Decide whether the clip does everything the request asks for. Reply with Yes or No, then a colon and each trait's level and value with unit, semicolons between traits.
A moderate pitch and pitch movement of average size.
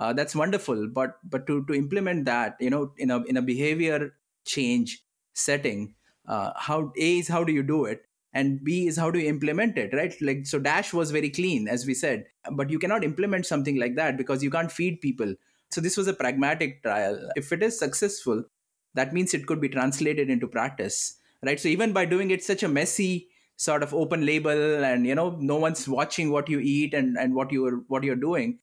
Yes: medium, 150 Hz; average, 4.1 semitones